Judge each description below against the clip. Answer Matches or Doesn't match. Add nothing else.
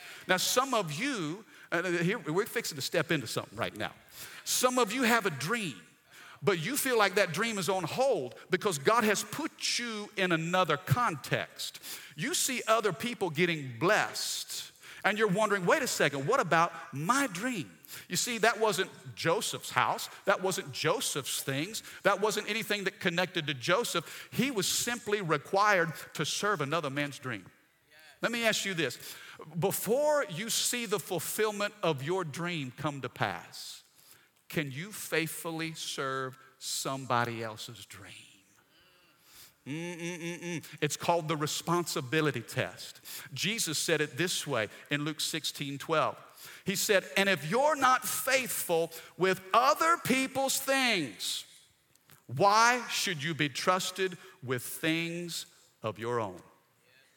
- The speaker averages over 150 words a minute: Doesn't match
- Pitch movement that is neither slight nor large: Doesn't match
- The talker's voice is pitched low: Doesn't match